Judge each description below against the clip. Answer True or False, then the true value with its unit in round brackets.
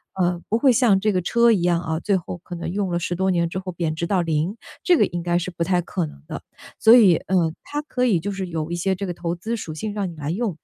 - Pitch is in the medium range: True (180 Hz)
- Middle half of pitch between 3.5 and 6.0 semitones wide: False (3.0 semitones)